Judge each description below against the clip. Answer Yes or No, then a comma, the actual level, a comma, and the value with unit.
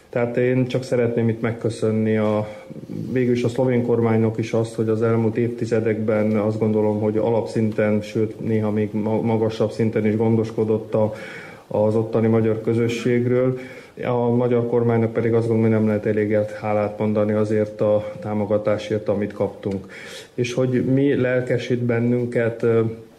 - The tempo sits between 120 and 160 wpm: Yes, average, 140 wpm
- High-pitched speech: No, low, 115 Hz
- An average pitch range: No, narrow, 1.8 semitones